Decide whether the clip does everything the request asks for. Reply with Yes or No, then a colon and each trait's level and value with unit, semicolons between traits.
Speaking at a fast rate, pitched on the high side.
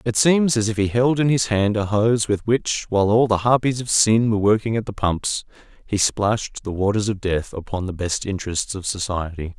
No: fast, 225 wpm; low, 105 Hz